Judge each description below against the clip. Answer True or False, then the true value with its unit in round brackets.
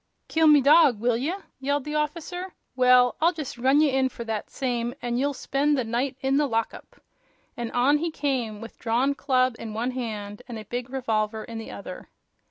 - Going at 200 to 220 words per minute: True (205 wpm)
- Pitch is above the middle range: True (255 Hz)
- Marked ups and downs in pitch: False (3.7 semitones)